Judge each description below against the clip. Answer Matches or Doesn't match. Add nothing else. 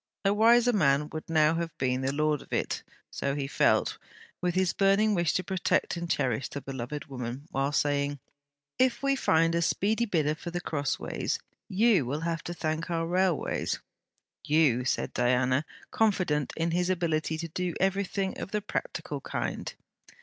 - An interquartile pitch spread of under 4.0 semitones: Doesn't match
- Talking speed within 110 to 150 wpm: Doesn't match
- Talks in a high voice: Doesn't match